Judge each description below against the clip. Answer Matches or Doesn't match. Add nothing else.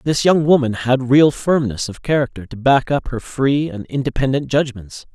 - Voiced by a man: Matches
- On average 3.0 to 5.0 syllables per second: Matches